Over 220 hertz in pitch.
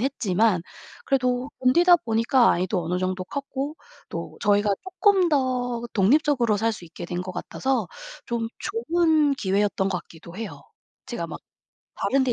Yes: high, 235 Hz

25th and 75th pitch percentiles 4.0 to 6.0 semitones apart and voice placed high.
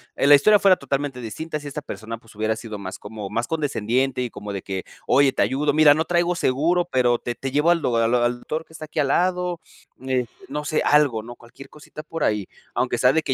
No: average, 4.7 semitones; low, 135 Hz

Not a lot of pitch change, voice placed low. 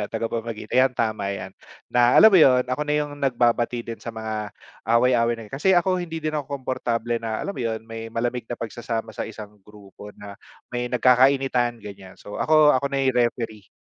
No: average, 3.0 semitones; low, 120 Hz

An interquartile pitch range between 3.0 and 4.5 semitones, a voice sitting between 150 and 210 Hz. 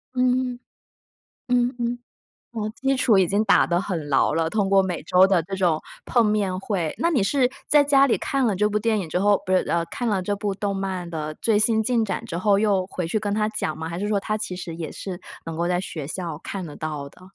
Yes: average, 3.9 semitones; high, 195 Hz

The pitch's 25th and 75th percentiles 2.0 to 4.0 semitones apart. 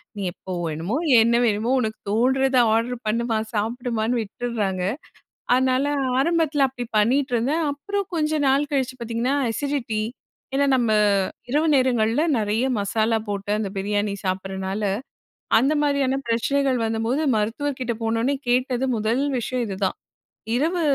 Yes: average, 3.6 semitones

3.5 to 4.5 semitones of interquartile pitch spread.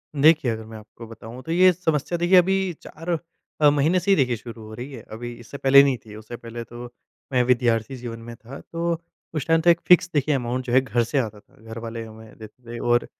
No: average, 5.0 semitones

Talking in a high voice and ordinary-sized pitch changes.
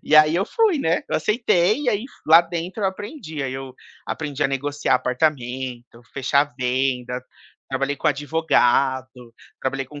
No: medium, 145 Hz; average, 4.4 semitones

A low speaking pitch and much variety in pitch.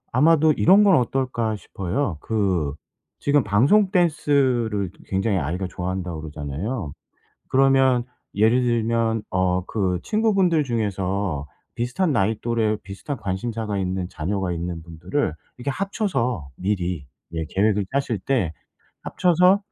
Yes: low, 110 Hz; wide, 6.6 semitones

